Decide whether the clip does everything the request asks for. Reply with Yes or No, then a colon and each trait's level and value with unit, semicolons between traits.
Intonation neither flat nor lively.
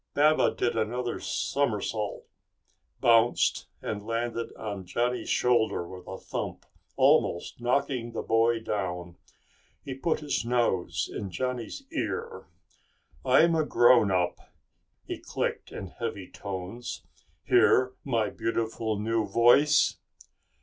Yes: average, 3.3 semitones